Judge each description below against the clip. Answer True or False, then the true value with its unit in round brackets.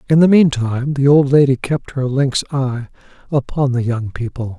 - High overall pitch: False (135 Hz)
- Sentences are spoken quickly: False (195 wpm)